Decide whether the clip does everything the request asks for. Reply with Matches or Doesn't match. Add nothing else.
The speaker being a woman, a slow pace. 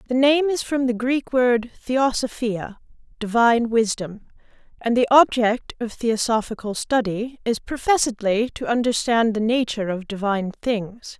Matches